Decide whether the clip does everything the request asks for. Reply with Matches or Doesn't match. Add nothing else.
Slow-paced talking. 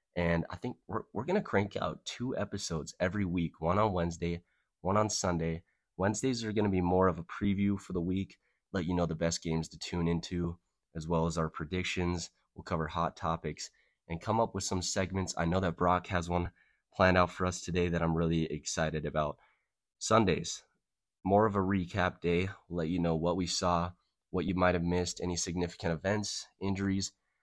Doesn't match